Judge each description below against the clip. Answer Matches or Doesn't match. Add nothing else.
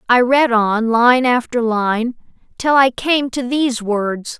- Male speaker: Doesn't match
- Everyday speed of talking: Matches